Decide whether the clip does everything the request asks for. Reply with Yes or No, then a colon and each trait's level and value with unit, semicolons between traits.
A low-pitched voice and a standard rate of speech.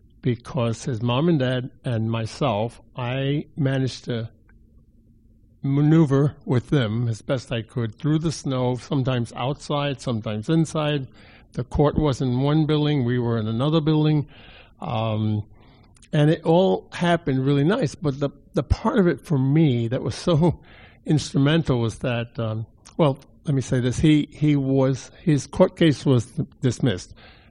Yes: low, 130 Hz; average, 155 wpm